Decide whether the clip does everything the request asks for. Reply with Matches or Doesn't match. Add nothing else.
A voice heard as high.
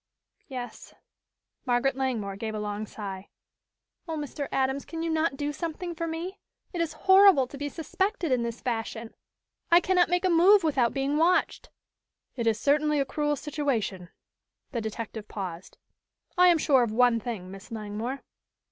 Matches